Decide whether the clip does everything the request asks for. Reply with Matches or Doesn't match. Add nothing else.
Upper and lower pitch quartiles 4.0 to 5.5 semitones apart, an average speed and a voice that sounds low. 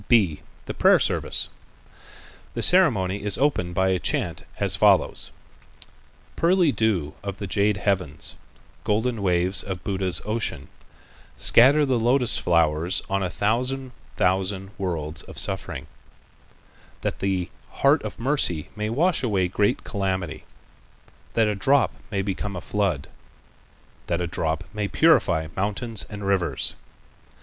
Doesn't match